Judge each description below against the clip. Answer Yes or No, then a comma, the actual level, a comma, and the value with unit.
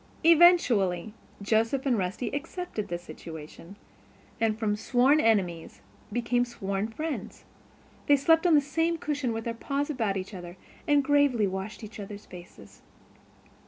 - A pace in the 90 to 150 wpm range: Yes, average, 140 wpm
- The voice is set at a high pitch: Yes, high, 225 Hz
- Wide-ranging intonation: Yes, wide, 6.6 semitones